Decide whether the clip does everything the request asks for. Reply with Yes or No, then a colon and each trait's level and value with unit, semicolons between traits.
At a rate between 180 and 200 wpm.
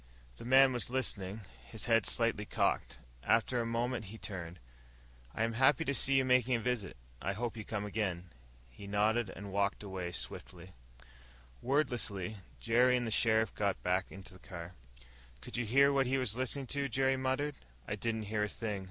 Yes: average, 185 wpm